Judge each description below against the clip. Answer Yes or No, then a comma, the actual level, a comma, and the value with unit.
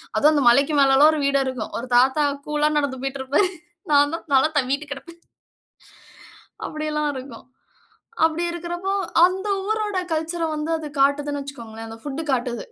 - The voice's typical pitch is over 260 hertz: Yes, very high, 290 Hz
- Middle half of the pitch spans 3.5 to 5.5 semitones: No, average, 3.1 semitones